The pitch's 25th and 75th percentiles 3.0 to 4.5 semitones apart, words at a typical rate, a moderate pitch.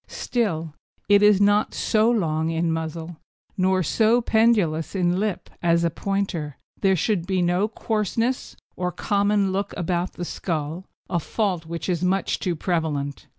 Yes: average, 3.7 semitones; average, 150 wpm; medium, 180 Hz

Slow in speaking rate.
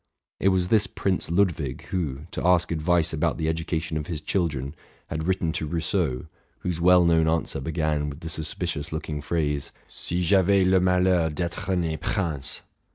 No: average, 175 wpm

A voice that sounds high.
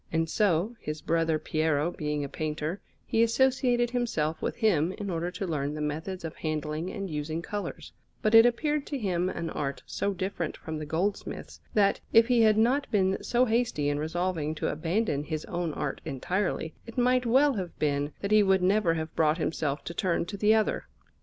No: medium, 175 Hz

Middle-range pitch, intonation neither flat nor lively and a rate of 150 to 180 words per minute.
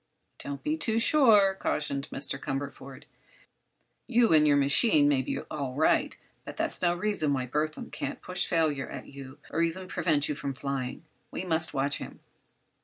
Yes: medium, 150 Hz; average, 4.6 semitones; average, 170 wpm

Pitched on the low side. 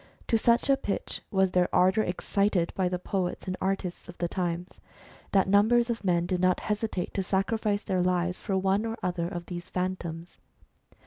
No: medium, 185 Hz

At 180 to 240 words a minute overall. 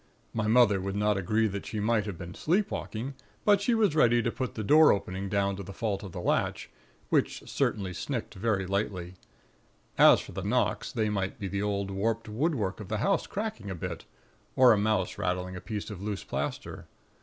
Yes: average, 200 wpm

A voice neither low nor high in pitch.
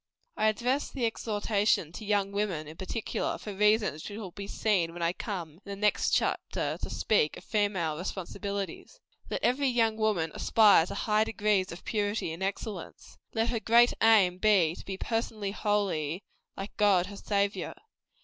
No: high, 205 Hz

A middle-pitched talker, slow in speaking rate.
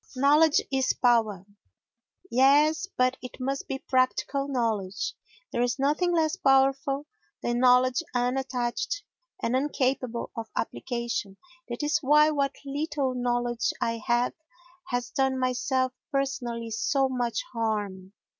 No: very high, 255 Hz; slow, 120 wpm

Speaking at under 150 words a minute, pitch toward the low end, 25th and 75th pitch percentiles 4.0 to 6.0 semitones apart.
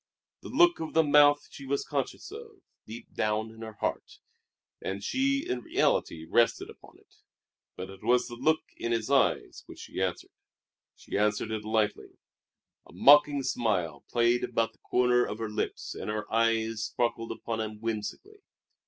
No: average, 170 wpm; low, 115 Hz; average, 4.7 semitones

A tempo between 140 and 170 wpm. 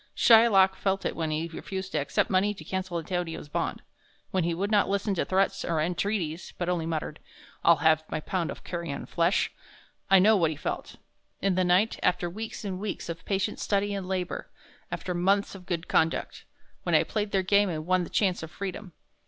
No: average, 200 wpm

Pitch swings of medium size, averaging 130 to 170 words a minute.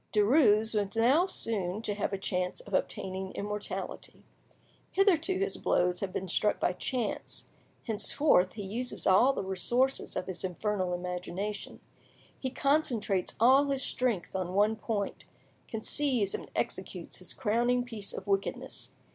Yes: average, 4.7 semitones; average, 140 wpm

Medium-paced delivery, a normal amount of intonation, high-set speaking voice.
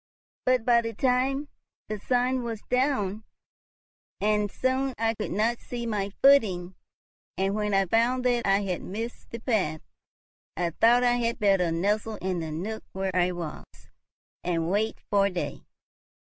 Yes: average, 155 wpm; average, 4.0 semitones; high, 215 Hz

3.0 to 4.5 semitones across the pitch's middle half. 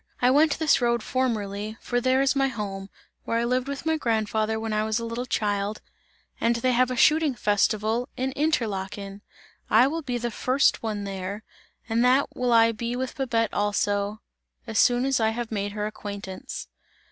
Yes: average, 3.4 semitones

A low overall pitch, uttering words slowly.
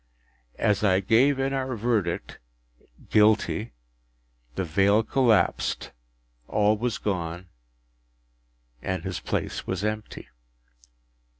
Yes: low, 105 Hz; slow, 95 wpm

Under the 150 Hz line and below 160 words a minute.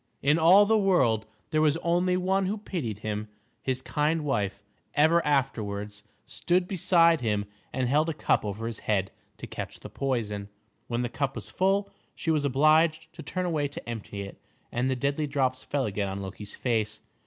No: medium, 140 Hz; average, 185 wpm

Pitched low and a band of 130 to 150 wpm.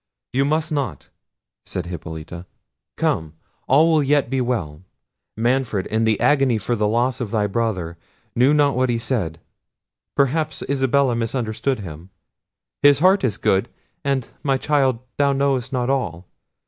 Yes: low, 125 Hz; average, 140 wpm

